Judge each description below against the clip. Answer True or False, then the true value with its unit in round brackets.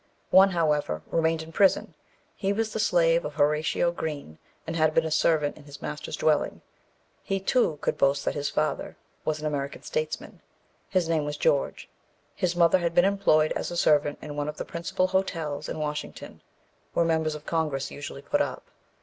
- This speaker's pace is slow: False (185 wpm)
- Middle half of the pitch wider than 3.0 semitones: False (2.7 semitones)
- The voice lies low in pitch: False (155 Hz)